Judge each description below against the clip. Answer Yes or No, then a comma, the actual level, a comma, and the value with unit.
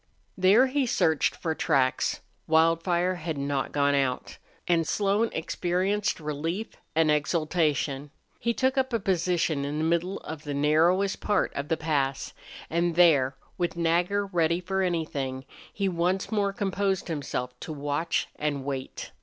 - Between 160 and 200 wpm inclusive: No, average, 145 wpm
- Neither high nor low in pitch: Yes, medium, 165 Hz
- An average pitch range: Yes, average, 4.3 semitones